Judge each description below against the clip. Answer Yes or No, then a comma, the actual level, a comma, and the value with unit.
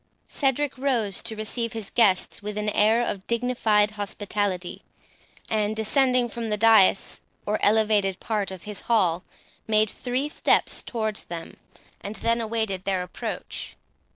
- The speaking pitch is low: No, high, 215 Hz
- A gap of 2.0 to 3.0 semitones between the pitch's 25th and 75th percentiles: Yes, narrow, 2.4 semitones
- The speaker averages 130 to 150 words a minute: Yes, average, 140 wpm